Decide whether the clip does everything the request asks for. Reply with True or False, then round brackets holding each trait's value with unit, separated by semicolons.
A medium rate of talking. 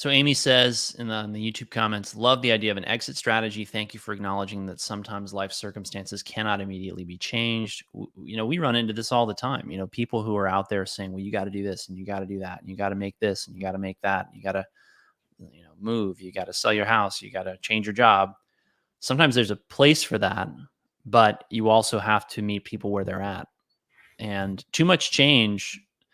False (250 wpm)